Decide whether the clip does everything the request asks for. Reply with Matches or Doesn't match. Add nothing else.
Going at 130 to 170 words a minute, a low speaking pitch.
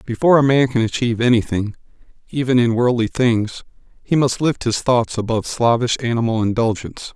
Matches